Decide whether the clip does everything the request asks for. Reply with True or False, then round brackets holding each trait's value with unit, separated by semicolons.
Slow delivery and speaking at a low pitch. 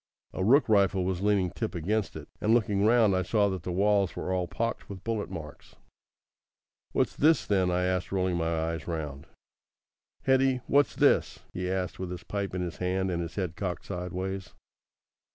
False (185 wpm; 95 Hz)